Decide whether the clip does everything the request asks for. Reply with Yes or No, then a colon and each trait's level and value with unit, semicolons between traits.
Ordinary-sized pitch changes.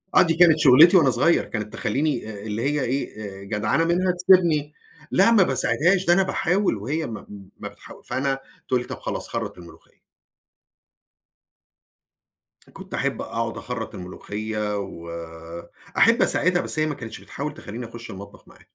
No: wide, 7.7 semitones